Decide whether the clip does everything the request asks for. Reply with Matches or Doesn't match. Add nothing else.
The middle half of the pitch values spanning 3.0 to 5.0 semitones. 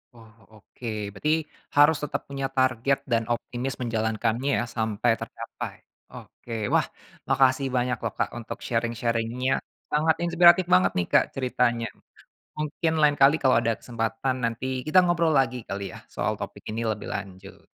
Matches